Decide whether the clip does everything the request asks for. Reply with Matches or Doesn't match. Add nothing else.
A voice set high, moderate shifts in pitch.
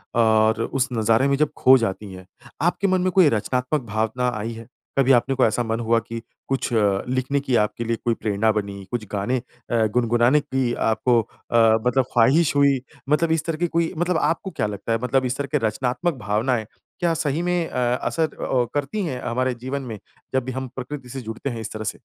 Doesn't match